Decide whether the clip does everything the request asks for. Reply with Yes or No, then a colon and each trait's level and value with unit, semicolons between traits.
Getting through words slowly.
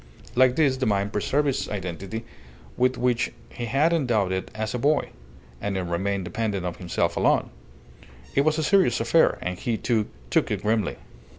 No: average, 180 wpm